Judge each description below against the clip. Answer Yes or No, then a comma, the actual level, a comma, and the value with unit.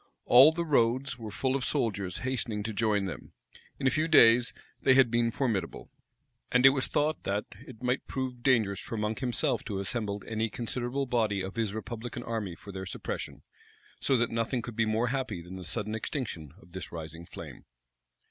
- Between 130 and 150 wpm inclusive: No, average, 195 wpm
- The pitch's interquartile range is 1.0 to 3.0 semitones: No, average, 3.9 semitones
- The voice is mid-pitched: No, low, 115 Hz